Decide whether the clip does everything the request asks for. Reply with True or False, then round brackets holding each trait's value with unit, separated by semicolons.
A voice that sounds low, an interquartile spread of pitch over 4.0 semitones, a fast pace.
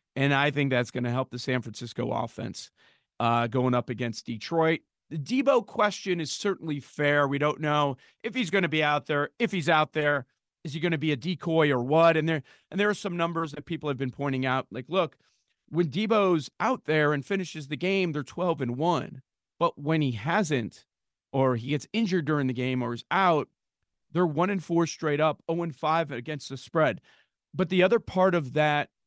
False (150 Hz; 4.4 semitones; 215 wpm)